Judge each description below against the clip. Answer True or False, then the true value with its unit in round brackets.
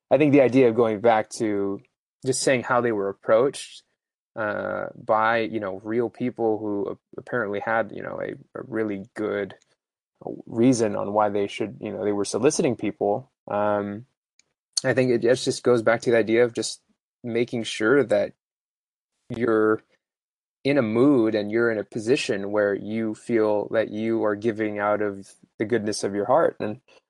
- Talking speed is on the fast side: False (175 wpm)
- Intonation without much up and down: True (2.3 semitones)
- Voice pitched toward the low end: True (110 Hz)